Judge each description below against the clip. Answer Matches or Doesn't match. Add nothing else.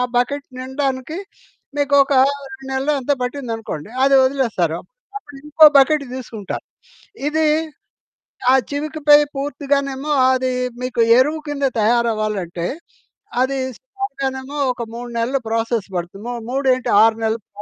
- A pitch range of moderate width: Matches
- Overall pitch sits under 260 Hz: Doesn't match